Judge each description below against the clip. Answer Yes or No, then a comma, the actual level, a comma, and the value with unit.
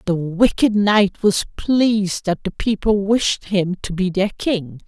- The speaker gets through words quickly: No, average, 170 wpm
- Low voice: No, high, 195 Hz